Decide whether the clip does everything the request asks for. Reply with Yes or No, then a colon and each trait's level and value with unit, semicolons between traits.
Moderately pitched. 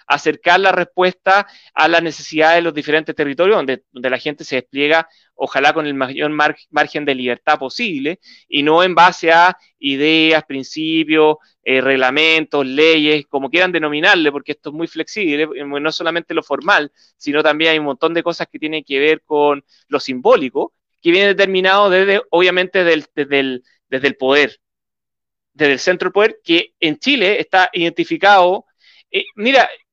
Yes: medium, 155 Hz